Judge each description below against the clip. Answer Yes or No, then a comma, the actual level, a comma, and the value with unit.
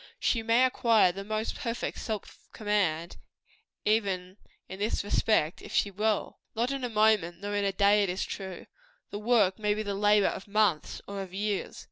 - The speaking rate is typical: Yes, average, 185 wpm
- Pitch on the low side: No, high, 205 Hz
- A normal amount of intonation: No, narrow, 2.1 semitones